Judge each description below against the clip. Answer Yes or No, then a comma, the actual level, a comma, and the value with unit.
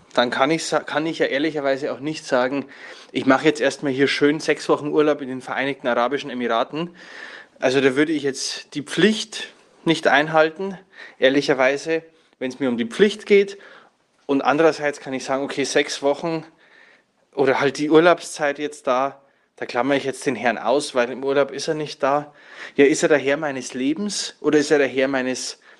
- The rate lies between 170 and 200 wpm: Yes, fast, 190 wpm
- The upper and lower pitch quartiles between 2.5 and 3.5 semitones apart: Yes, average, 2.8 semitones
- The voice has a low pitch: No, medium, 145 Hz